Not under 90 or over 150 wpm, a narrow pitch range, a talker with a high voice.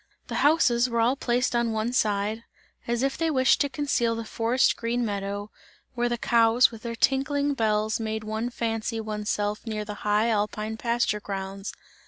No: average, 180 wpm; narrow, 2.2 semitones; high, 230 Hz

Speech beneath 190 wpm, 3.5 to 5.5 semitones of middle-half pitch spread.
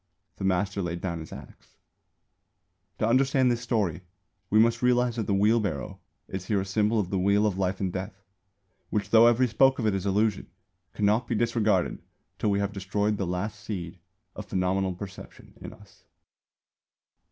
No: average, 175 wpm; average, 2.9 semitones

